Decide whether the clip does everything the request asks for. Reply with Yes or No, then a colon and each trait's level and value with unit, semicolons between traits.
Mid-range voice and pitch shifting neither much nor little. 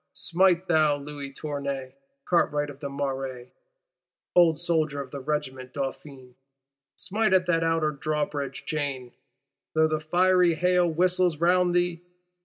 Yes: medium, 155 Hz; average, 3.9 semitones